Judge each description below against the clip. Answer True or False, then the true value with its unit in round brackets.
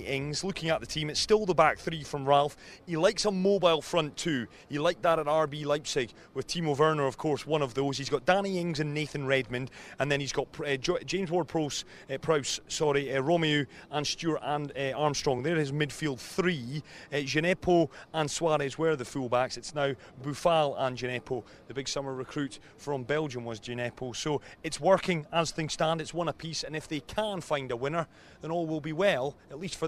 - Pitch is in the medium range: True (150 Hz)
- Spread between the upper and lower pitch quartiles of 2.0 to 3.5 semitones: True (3.1 semitones)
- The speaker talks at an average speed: False (210 wpm)